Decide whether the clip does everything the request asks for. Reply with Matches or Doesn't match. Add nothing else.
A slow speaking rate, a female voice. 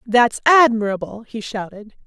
Matches